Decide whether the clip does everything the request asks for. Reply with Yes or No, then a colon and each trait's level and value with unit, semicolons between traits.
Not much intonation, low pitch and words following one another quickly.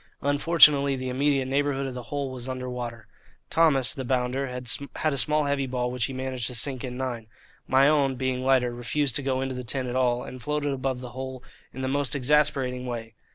Yes: narrow, 1.8 semitones; low, 130 Hz; fast, 210 wpm